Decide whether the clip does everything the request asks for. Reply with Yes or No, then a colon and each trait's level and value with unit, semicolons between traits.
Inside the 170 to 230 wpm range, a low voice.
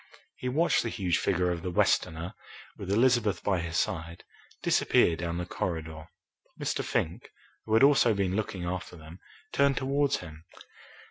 No: average, 155 wpm; very low, 90 Hz